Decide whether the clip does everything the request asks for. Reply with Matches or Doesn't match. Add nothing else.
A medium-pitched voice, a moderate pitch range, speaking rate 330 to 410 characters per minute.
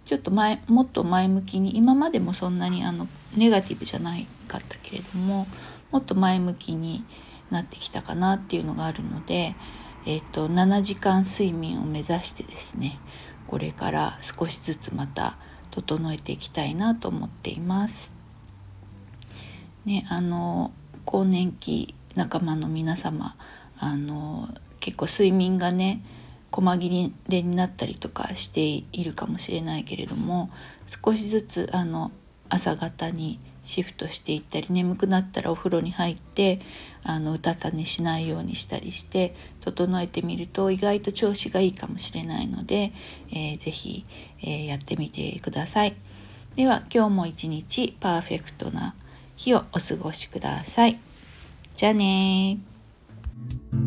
Doesn't match